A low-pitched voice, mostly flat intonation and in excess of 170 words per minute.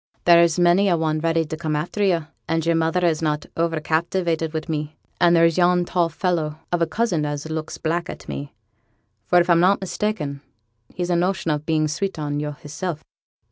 No: medium, 165 Hz; narrow, 2.2 semitones; average, 200 wpm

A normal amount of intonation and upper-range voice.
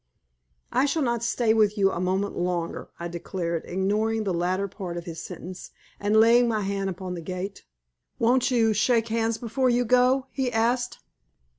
Yes: average, 4.4 semitones; high, 215 Hz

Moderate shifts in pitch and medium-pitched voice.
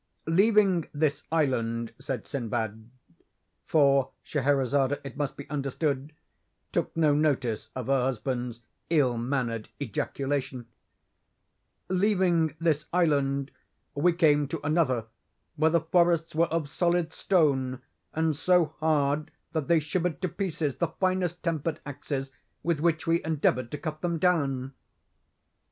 Yes: average, 3.6 semitones; medium, 150 Hz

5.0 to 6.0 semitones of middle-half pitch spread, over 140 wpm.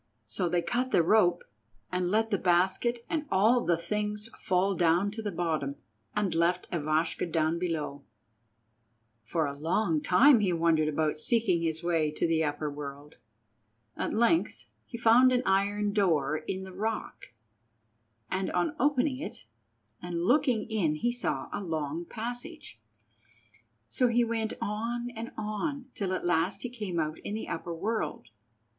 Yes: wide, 5.5 semitones; average, 155 wpm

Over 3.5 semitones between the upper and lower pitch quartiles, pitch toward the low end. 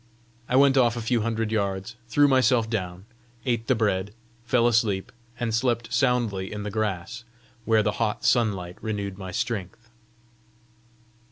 No: average, 3.0 semitones; low, 110 Hz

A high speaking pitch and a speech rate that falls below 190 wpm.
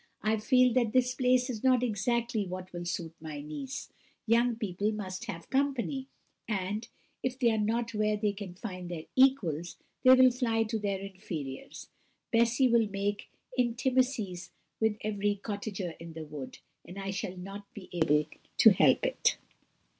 Yes: high, 210 Hz; average, 160 wpm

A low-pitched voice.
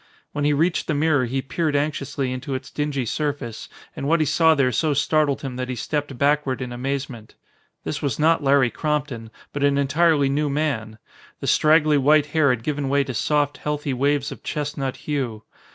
No: medium, 145 Hz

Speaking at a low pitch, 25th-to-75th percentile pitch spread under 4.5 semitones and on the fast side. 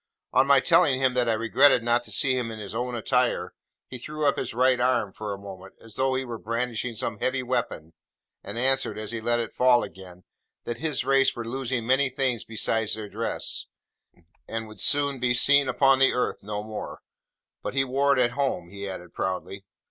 Yes: low, 120 Hz; average, 3.4 semitones; fast, 210 wpm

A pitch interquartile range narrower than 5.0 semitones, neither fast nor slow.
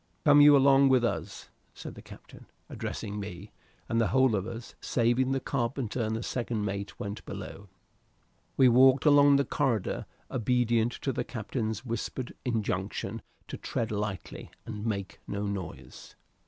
Yes: average, 4.0 semitones; average, 150 wpm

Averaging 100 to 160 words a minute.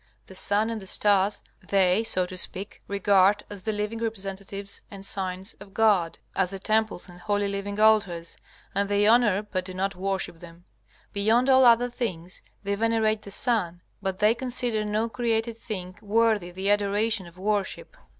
No: average, 170 wpm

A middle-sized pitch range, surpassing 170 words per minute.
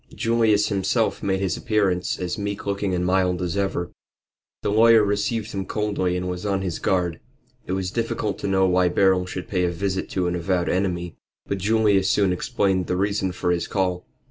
No: narrow, 2.0 semitones; average, 195 wpm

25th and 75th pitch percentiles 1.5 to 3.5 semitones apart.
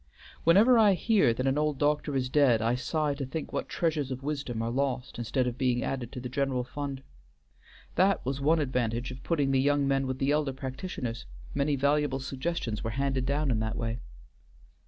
Yes: average, 2.7 semitones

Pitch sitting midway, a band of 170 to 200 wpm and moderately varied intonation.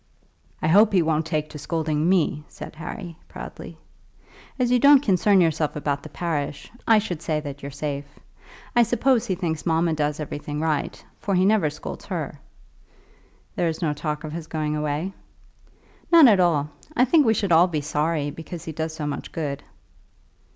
Yes: medium, 160 Hz; average, 180 wpm; average, 3.7 semitones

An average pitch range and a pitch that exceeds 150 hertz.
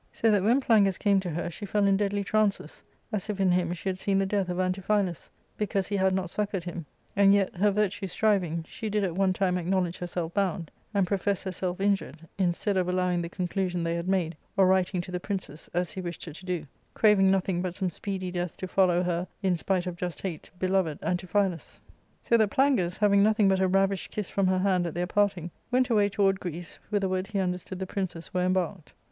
No: narrow, 2.0 semitones; medium, 185 Hz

